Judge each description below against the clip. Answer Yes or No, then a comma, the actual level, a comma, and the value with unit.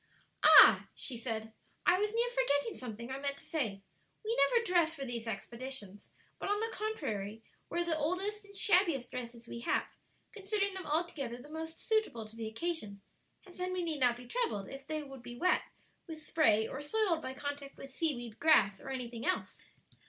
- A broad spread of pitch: Yes, wide, 7.4 semitones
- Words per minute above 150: Yes, average, 190 wpm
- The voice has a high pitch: Yes, very high, 285 Hz